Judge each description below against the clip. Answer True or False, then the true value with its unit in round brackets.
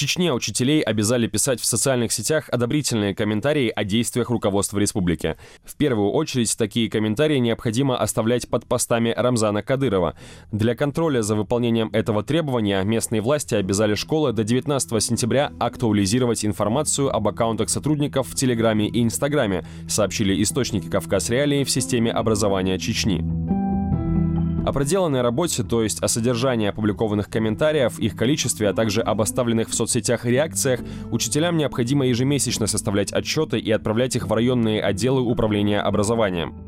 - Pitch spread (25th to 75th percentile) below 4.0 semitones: True (3.3 semitones)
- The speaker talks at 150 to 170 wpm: False (140 wpm)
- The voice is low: True (115 Hz)